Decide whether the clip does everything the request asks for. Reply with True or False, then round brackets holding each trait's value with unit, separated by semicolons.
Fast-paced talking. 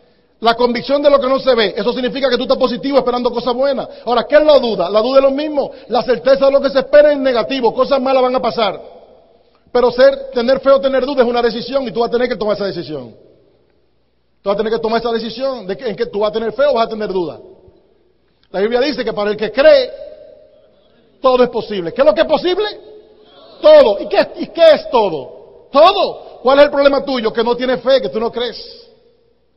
True (245 wpm)